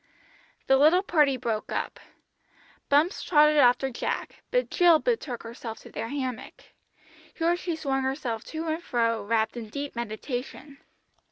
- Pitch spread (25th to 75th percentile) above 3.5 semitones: Yes, average, 5.0 semitones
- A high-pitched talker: Yes, very high, 270 Hz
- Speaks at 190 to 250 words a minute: No, average, 145 wpm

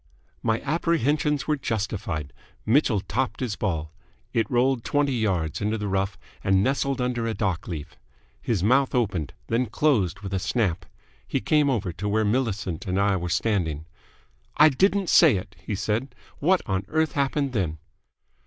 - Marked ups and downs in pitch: Yes, wide, 5.9 semitones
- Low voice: Yes, low, 110 Hz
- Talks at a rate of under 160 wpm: No, average, 165 wpm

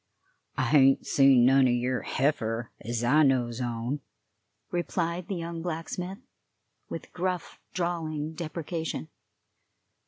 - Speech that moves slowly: Yes, slow, 115 wpm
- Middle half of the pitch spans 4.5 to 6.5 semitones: Yes, average, 5.3 semitones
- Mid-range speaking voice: Yes, medium, 145 Hz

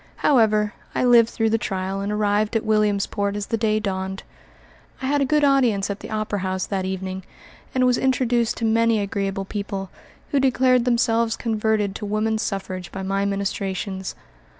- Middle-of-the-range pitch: No, high, 210 Hz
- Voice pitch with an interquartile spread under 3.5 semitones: Yes, average, 2.8 semitones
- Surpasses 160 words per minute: Yes, average, 175 wpm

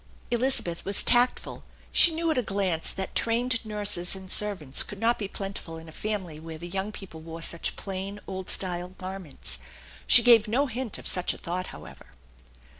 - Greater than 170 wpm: Yes, average, 185 wpm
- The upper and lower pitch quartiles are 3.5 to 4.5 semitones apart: Yes, average, 4.2 semitones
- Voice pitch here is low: No, high, 195 Hz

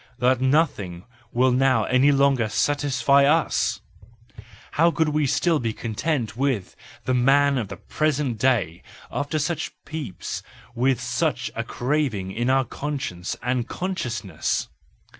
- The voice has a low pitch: Yes, low, 130 Hz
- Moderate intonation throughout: Yes, average, 3.7 semitones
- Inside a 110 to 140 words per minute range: Yes, slow, 135 wpm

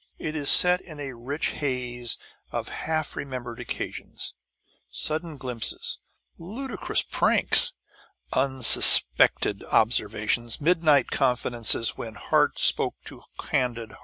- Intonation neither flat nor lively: Yes, average, 4.7 semitones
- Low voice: Yes, low, 130 Hz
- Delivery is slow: Yes, slow, 105 wpm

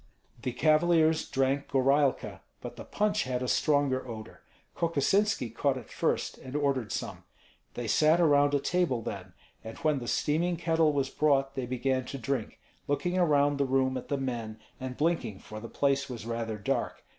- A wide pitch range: No, average, 3.4 semitones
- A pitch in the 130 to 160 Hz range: Yes, low, 135 Hz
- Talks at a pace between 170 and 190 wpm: Yes, average, 175 wpm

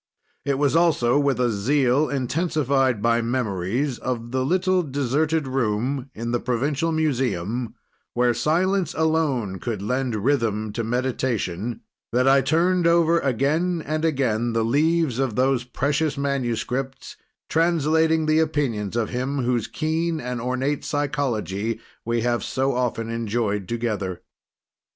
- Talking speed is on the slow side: Yes, slow, 130 wpm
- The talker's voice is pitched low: Yes, low, 130 Hz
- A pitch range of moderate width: Yes, average, 4.4 semitones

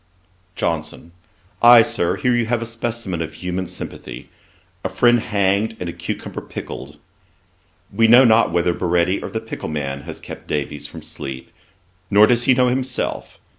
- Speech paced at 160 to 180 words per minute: Yes, average, 165 wpm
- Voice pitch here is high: No, low, 100 Hz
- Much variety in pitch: Yes, wide, 5.8 semitones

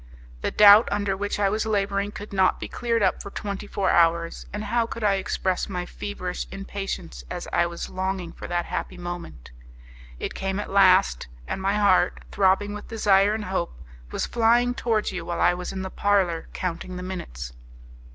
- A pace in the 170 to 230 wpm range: Yes, average, 190 wpm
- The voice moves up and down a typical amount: No, narrow, 2.3 semitones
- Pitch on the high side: Yes, high, 195 Hz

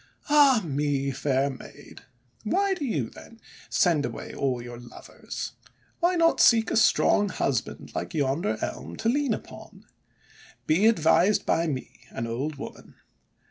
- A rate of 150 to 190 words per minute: No, average, 140 wpm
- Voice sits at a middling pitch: Yes, medium, 160 Hz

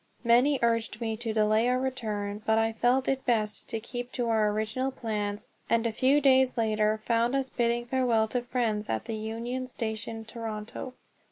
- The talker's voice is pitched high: Yes, high, 230 Hz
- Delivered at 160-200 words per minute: Yes, average, 180 wpm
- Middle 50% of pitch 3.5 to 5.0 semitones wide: No, narrow, 2.4 semitones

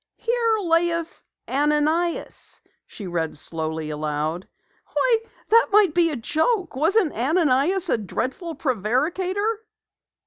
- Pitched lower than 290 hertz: No, very high, 315 Hz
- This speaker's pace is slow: Yes, slow, 105 wpm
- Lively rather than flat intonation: Yes, wide, 8.7 semitones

